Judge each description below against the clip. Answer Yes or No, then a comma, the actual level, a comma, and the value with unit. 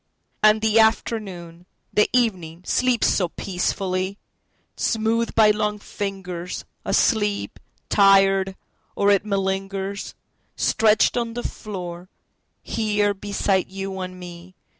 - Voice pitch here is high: Yes, high, 195 Hz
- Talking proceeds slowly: Yes, slow, 95 wpm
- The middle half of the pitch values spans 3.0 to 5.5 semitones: No, narrow, 2.4 semitones